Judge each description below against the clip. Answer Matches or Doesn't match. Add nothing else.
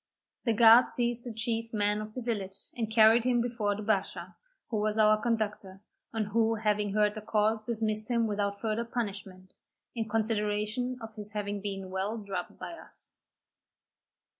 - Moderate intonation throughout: Doesn't match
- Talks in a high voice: Matches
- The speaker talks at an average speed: Matches